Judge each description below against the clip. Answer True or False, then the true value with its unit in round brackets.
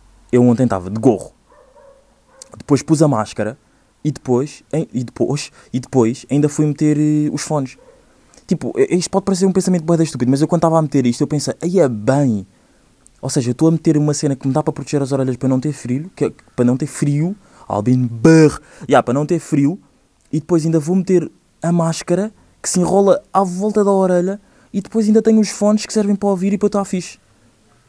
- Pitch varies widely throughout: True (5.9 semitones)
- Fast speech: True (210 wpm)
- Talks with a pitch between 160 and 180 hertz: False (150 Hz)